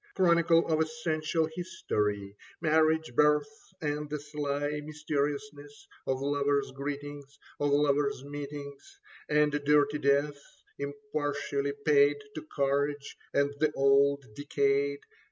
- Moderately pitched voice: Yes, medium, 145 Hz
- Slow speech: Yes, slow, 105 wpm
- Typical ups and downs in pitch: No, narrow, 1.1 semitones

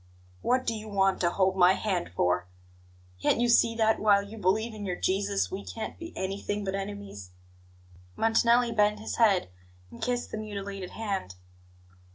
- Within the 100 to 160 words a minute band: No, average, 170 wpm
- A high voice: Yes, high, 205 Hz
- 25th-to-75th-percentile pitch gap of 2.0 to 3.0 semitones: Yes, narrow, 2.6 semitones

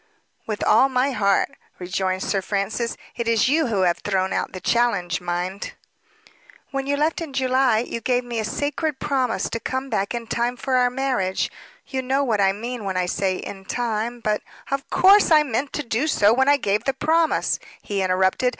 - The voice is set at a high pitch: Yes, high, 235 Hz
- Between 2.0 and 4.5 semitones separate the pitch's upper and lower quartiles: No, average, 5.1 semitones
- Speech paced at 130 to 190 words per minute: No, average, 200 wpm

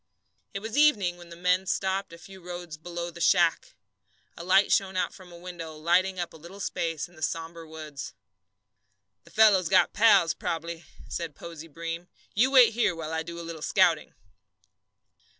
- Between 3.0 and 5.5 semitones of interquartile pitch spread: No, narrow, 2.5 semitones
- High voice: No, medium, 175 Hz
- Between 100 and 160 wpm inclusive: No, average, 180 wpm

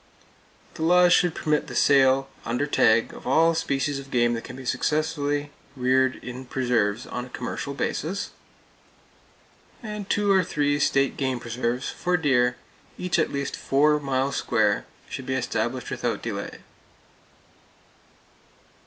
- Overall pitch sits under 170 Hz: Yes, medium, 140 Hz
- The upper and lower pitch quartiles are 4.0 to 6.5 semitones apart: No, average, 3.3 semitones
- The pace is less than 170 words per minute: Yes, slow, 135 wpm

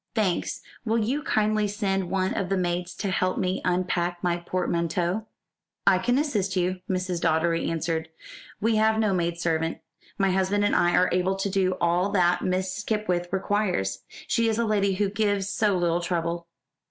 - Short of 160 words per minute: No, average, 175 wpm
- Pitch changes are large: No, average, 2.8 semitones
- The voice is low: No, medium, 185 Hz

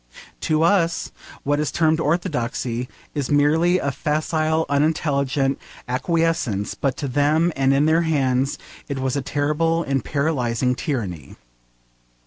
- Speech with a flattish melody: No, average, 3.3 semitones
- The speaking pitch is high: No, medium, 145 Hz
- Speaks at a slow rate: Yes, slow, 125 wpm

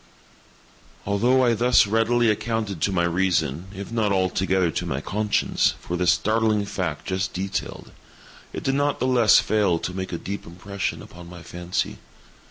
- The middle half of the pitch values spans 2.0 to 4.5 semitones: Yes, average, 3.8 semitones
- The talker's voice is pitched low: Yes, low, 100 Hz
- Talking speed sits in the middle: Yes, average, 165 wpm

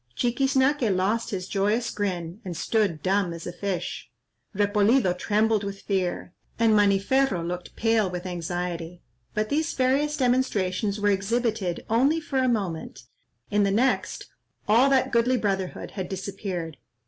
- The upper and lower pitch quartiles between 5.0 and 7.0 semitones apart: No, average, 4.4 semitones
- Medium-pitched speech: No, high, 205 Hz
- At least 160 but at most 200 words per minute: No, slow, 135 wpm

